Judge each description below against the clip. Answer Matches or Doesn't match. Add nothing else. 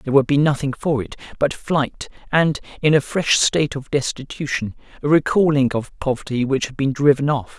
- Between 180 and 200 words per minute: Matches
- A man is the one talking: Matches